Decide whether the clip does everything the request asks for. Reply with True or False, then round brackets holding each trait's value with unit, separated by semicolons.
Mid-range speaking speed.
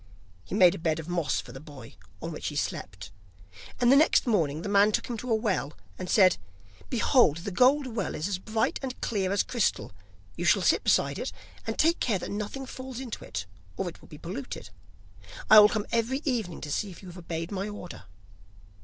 False (215 wpm)